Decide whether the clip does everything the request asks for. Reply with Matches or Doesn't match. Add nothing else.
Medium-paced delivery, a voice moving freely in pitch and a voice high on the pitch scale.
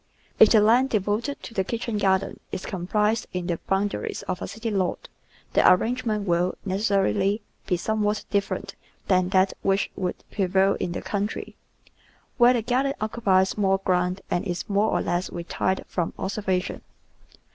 Doesn't match